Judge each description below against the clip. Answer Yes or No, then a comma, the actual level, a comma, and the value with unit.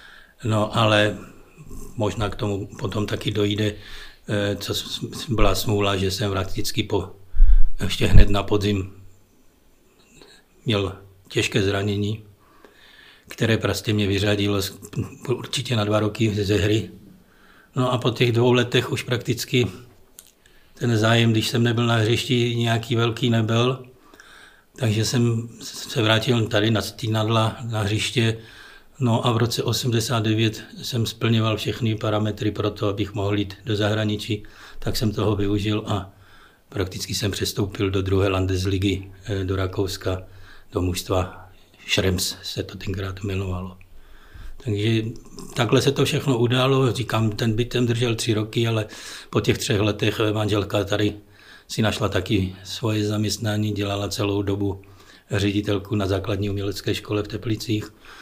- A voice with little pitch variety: Yes, narrow, 2.3 semitones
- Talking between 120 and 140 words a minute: Yes, average, 135 wpm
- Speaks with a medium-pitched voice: No, low, 105 Hz